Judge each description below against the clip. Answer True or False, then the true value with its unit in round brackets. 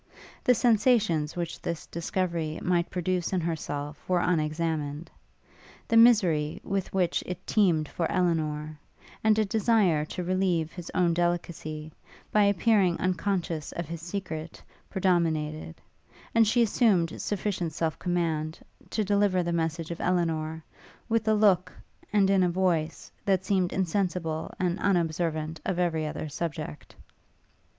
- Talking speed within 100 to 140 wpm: True (135 wpm)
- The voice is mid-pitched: True (175 Hz)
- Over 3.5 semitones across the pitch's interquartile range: False (3.2 semitones)